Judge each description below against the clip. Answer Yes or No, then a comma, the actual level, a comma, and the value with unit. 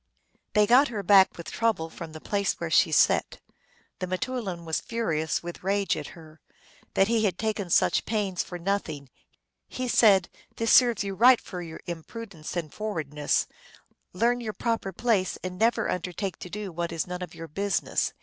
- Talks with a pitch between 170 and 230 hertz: Yes, high, 190 Hz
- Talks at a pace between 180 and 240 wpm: Yes, average, 185 wpm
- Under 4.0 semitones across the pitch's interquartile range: No, average, 4.5 semitones